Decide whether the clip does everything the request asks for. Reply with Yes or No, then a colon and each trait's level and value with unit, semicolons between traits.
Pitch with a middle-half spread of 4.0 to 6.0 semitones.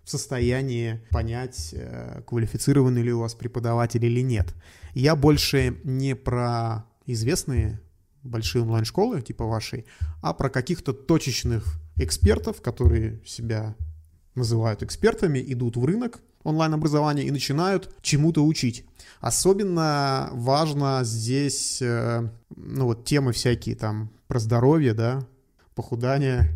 No: average, 3.4 semitones